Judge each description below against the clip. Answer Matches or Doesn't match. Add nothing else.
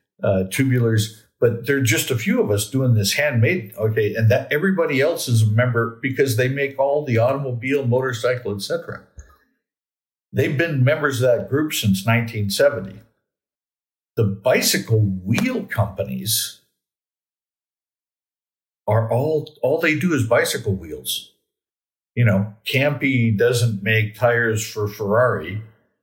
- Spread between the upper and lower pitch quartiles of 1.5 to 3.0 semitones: Doesn't match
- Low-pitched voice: Matches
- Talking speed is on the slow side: Matches